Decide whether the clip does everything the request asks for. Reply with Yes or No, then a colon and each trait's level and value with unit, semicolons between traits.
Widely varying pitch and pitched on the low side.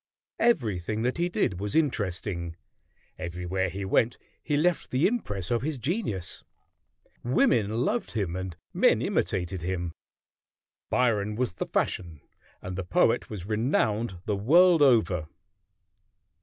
Yes: wide, 5.7 semitones; low, 105 Hz